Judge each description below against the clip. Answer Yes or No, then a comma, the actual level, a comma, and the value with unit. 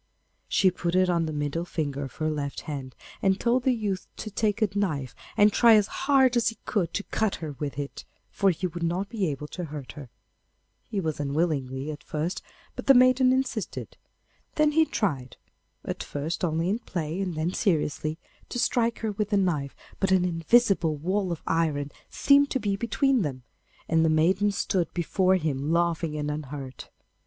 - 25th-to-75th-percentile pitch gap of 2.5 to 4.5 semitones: No, wide, 5.4 semitones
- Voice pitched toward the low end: No, medium, 175 Hz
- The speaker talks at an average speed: Yes, average, 190 wpm